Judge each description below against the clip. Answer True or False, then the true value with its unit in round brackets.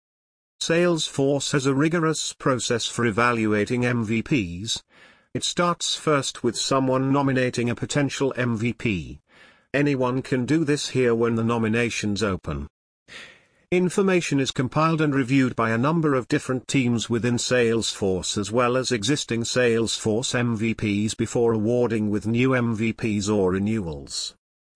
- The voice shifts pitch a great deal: False (3.4 semitones)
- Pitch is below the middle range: True (120 Hz)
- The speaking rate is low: True (125 wpm)